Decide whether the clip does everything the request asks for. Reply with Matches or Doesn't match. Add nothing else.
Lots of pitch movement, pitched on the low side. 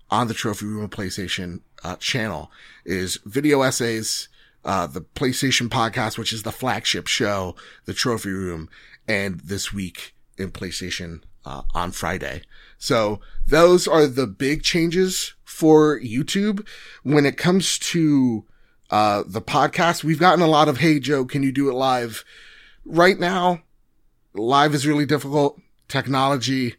Matches